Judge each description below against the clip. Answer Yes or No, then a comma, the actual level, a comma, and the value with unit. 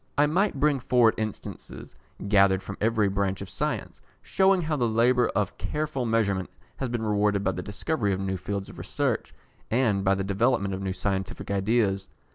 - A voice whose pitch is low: Yes, low, 105 Hz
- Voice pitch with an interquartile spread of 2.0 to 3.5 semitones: No, average, 4.0 semitones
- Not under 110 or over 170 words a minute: No, average, 180 wpm